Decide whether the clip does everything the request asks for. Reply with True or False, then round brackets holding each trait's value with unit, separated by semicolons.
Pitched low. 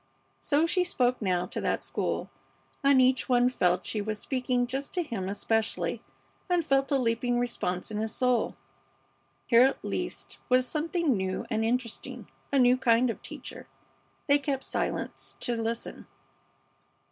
False (245 Hz)